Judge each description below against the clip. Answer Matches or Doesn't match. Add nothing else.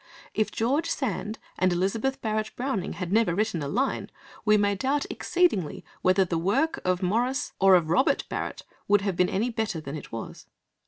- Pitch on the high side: Matches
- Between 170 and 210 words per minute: Matches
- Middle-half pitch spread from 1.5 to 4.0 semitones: Doesn't match